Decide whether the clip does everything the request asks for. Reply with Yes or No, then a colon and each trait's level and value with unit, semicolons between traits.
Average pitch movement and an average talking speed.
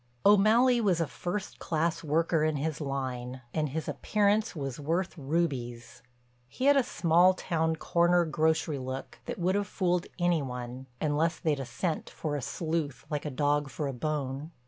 Yes: average, 4.0 semitones; average, 170 wpm